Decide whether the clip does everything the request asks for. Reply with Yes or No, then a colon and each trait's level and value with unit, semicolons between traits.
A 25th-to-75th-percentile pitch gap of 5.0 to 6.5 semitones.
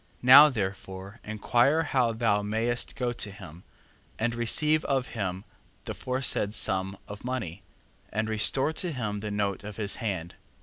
No: average, 4.0 semitones